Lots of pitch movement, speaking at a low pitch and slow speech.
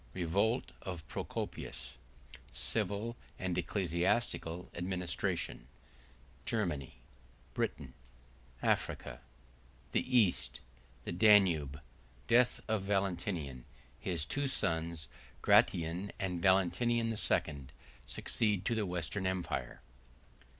Yes: wide, 7.0 semitones; very low, 85 Hz; slow, 70 wpm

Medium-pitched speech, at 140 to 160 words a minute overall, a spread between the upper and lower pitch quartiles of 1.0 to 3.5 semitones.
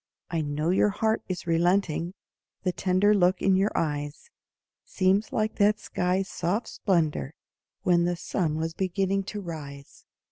Yes: medium, 180 Hz; average, 145 wpm; average, 3.1 semitones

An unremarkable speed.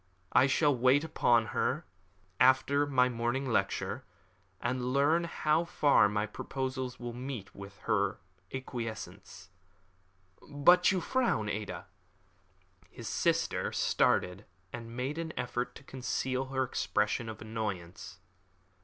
No: slow, 115 wpm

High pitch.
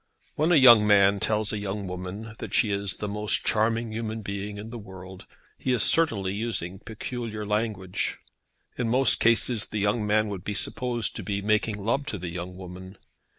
No: low, 105 Hz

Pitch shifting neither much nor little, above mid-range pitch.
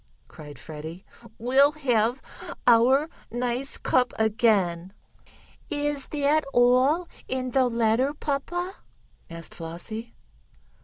Yes: average, 4.4 semitones; high, 245 Hz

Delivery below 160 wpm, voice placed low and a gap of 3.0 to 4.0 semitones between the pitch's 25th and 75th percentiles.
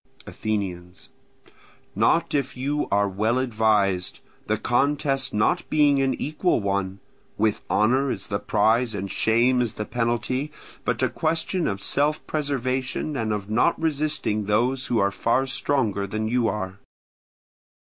No: average, 140 wpm; low, 115 Hz; average, 4.7 semitones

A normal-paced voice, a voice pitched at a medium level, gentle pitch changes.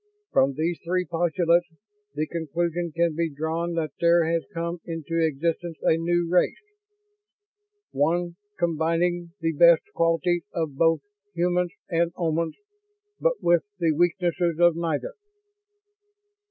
No: slow, 125 wpm; medium, 170 Hz; narrow, 1.1 semitones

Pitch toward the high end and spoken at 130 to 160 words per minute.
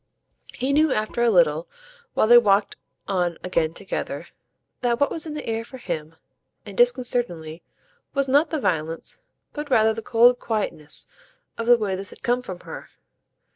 No: high, 230 Hz; average, 175 wpm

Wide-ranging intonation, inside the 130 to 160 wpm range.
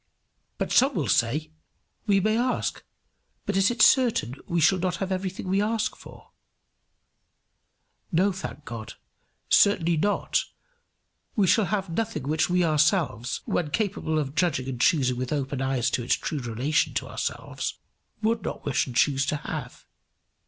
Yes: wide, 6.4 semitones; average, 155 wpm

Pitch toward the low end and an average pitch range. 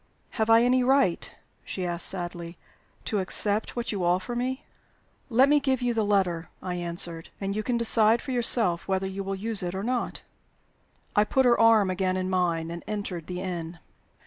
No: high, 195 Hz; average, 4.6 semitones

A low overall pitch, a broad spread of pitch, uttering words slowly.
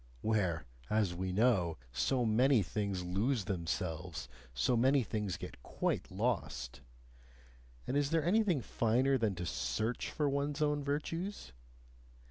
Yes: low, 110 Hz; wide, 7.5 semitones; slow, 130 wpm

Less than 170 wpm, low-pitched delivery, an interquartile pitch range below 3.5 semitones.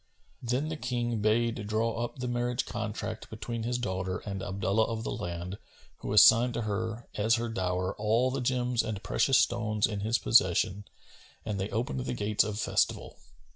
No: average, 175 wpm; low, 110 Hz; average, 2.8 semitones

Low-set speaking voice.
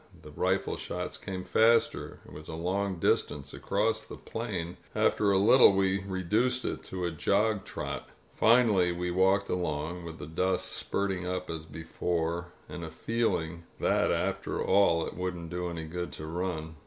Yes: very low, 90 Hz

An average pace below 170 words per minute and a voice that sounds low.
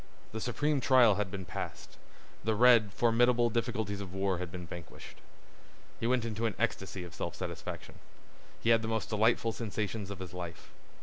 No: average, 175 wpm; low, 110 Hz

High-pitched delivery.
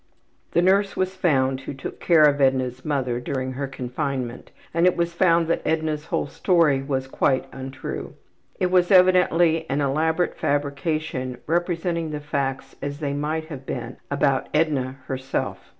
No: medium, 145 Hz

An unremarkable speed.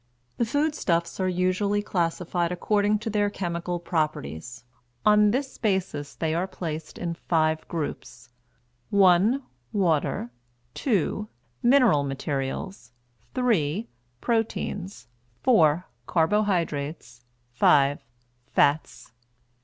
No: slow, 90 wpm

